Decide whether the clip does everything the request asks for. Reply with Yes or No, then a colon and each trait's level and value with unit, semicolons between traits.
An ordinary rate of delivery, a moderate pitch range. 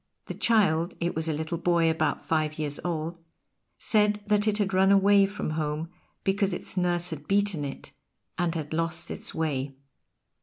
Yes: average, 175 wpm; average, 3.8 semitones